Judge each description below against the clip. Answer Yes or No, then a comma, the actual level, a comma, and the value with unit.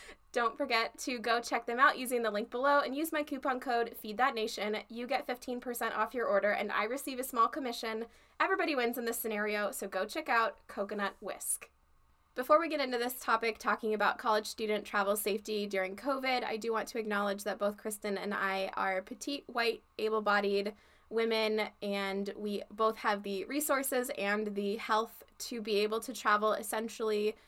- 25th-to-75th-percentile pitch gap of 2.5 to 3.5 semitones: Yes, average, 3.2 semitones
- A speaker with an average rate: Yes, average, 190 wpm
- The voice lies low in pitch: No, high, 225 Hz